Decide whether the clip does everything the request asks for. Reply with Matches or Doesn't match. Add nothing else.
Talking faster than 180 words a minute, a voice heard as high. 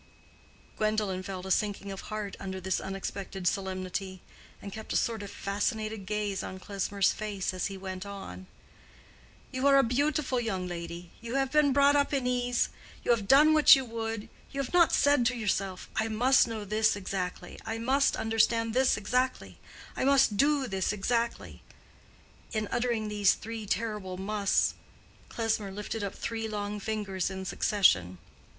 Doesn't match